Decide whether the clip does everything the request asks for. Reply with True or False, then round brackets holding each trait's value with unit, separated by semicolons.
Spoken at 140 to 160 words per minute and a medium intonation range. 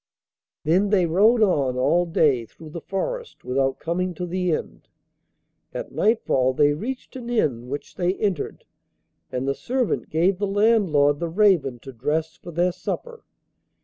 False (155 wpm; 6.0 semitones)